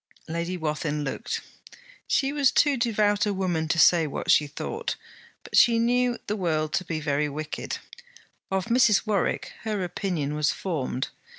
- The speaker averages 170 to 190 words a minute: No, average, 160 wpm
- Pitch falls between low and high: Yes, medium, 180 Hz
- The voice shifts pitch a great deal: Yes, wide, 5.9 semitones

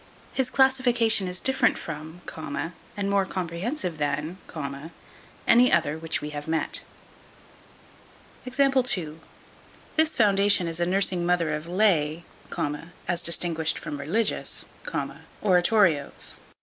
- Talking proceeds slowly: Yes, slow, 100 wpm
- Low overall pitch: No, medium, 180 Hz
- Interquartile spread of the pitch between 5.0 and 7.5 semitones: Yes, average, 5.3 semitones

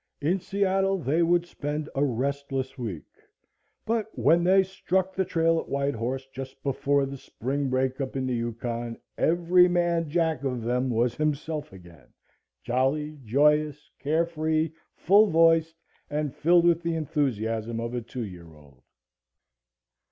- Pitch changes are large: No, average, 4.8 semitones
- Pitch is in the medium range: Yes, medium, 145 Hz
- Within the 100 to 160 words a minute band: Yes, average, 145 wpm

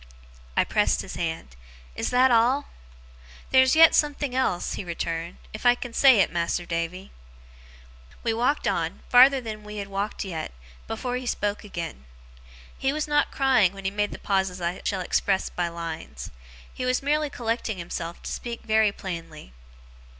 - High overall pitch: Yes, high, 210 Hz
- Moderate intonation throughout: No, wide, 6.3 semitones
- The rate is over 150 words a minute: Yes, average, 170 wpm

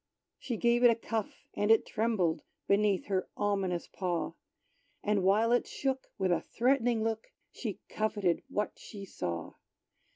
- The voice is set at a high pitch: Yes, high, 210 Hz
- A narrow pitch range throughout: No, average, 3.2 semitones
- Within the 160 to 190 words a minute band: No, average, 150 wpm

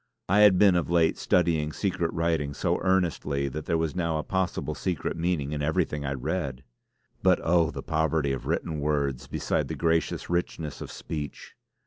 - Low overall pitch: Yes, very low, 80 Hz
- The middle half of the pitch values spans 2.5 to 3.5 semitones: Yes, average, 3.1 semitones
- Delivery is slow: No, average, 175 wpm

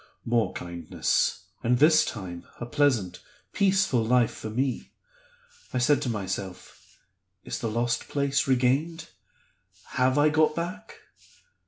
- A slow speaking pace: Yes, slow, 125 wpm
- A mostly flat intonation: No, average, 4.8 semitones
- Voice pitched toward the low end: Yes, low, 125 Hz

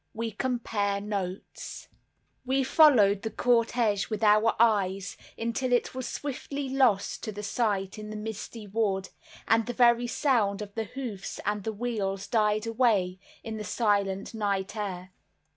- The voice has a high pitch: Yes, high, 215 Hz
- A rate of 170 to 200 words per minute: No, average, 145 wpm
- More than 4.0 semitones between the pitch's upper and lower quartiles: No, average, 3.0 semitones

